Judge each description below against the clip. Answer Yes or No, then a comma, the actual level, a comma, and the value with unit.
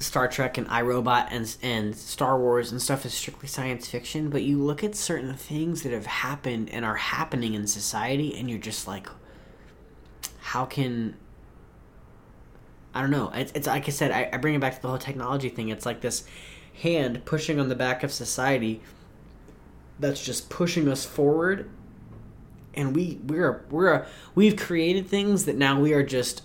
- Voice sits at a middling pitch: No, low, 130 Hz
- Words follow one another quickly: No, average, 180 wpm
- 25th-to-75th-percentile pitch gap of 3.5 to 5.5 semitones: Yes, average, 3.8 semitones